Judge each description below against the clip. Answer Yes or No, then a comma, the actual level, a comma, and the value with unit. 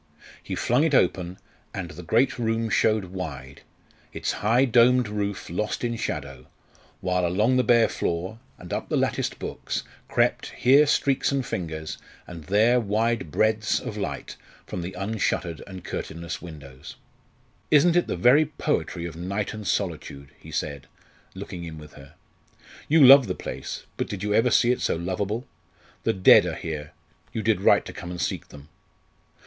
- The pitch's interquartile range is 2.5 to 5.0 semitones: No, wide, 5.6 semitones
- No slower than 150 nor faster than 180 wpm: Yes, average, 170 wpm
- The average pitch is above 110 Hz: No, low, 100 Hz